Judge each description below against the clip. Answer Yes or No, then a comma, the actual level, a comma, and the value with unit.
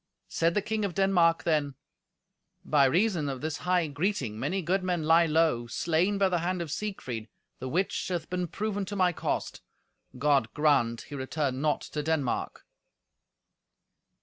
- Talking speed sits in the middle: Yes, average, 160 wpm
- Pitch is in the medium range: Yes, medium, 165 Hz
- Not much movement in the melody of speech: No, average, 4.4 semitones